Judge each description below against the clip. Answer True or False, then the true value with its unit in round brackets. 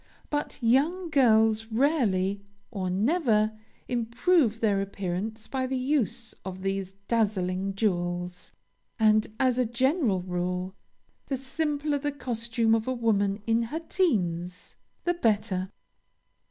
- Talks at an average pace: False (120 wpm)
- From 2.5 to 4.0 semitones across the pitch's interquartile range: False (5.1 semitones)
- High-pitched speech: True (225 Hz)